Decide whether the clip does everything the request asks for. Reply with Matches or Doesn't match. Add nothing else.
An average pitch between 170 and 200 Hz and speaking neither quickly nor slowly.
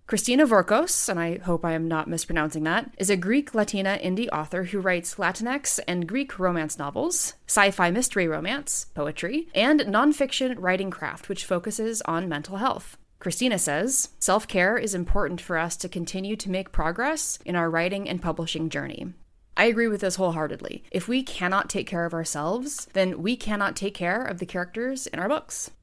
Matches